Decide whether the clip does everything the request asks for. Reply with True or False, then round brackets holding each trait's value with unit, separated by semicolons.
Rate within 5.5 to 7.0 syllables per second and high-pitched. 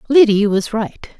False (4.4 syllables/s; 225 Hz)